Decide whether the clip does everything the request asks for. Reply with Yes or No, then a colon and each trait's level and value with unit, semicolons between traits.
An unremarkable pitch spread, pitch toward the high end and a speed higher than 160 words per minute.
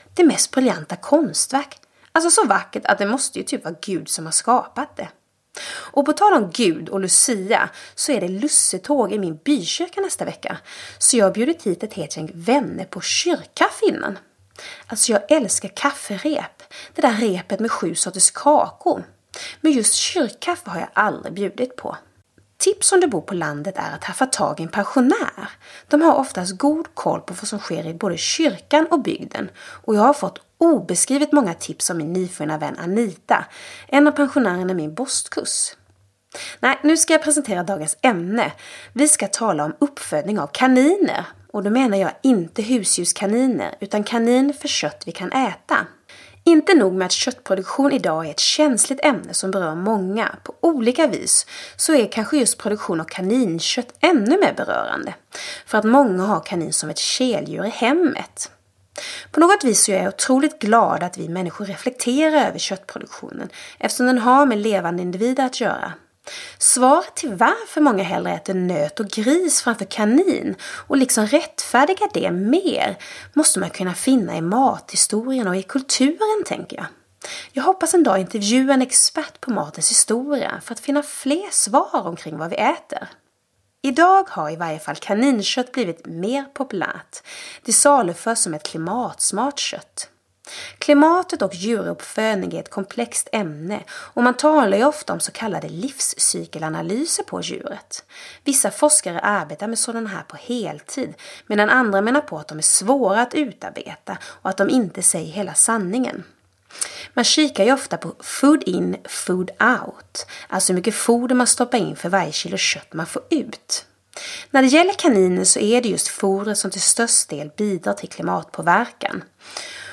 No: wide, 7.0 semitones; high, 240 Hz; average, 170 wpm